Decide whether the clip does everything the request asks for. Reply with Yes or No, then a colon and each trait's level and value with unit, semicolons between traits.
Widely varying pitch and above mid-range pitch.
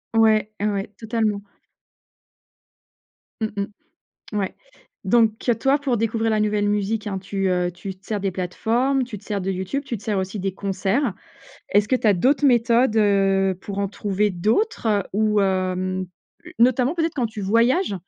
No: average, 3.0 semitones; high, 210 Hz